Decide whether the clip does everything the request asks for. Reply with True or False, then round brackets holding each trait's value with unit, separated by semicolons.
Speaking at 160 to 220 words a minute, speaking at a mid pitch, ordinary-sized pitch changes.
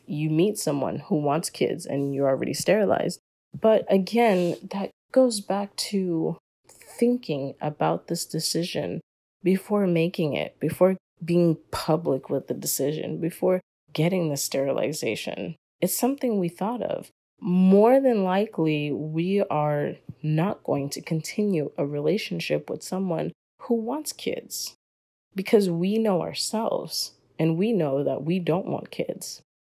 False (135 wpm; 175 Hz; 4.4 semitones)